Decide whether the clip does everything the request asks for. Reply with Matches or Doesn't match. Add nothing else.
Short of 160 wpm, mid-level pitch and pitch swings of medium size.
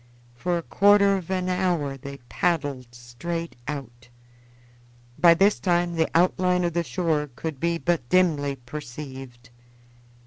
Matches